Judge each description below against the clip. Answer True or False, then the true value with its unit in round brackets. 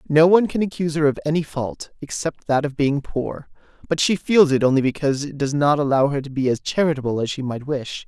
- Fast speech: True (240 wpm)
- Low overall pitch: False (145 Hz)